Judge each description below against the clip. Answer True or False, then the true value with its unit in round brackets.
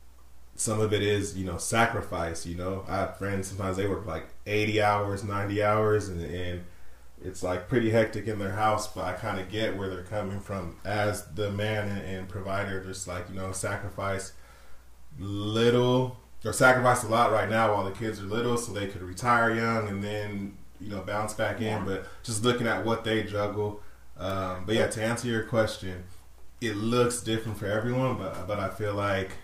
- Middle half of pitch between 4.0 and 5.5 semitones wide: False (2.6 semitones)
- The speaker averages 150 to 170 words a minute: False (200 wpm)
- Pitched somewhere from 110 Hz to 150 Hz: False (100 Hz)